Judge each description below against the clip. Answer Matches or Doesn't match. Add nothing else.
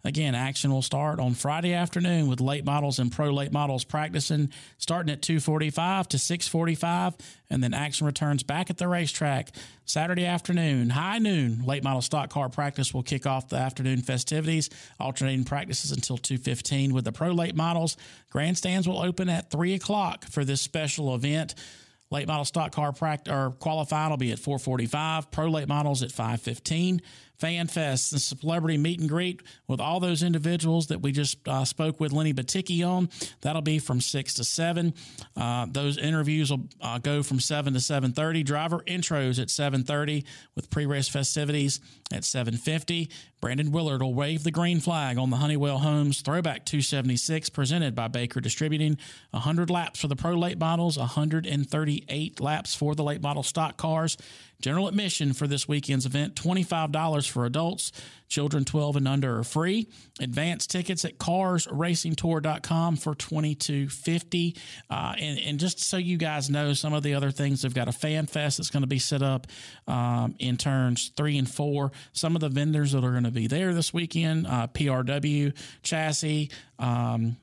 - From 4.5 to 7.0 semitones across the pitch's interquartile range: Doesn't match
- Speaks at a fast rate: Doesn't match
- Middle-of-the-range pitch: Matches